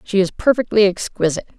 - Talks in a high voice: Yes, high, 195 Hz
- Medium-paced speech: Yes, average, 150 wpm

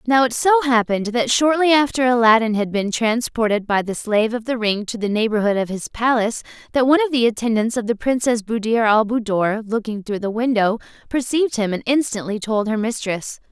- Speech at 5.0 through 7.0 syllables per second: Yes, 5.7 syllables/s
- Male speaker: No, female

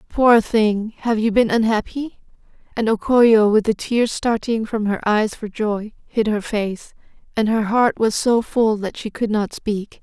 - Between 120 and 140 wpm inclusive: No, average, 190 wpm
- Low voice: No, high, 220 Hz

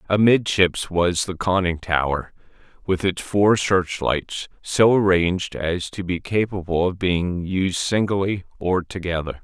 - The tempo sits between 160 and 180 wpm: No, slow, 135 wpm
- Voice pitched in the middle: No, very low, 90 Hz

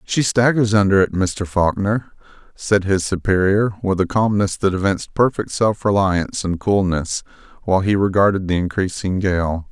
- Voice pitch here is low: Yes, very low, 95 Hz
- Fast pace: No, average, 155 wpm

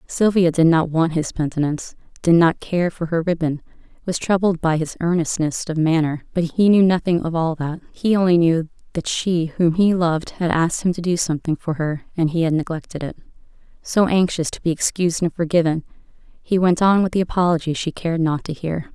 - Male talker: No, female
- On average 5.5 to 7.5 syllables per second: Yes, 5.6 syllables/s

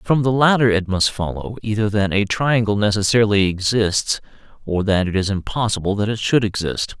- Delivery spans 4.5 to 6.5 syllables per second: Yes, 5.3 syllables/s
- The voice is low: Yes, low, 105 Hz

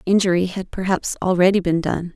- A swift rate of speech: No, average, 165 wpm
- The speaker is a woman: Yes, female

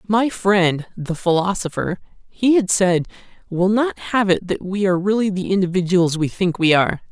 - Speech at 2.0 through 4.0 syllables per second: No, 4.9 syllables/s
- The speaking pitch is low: No, medium, 185 Hz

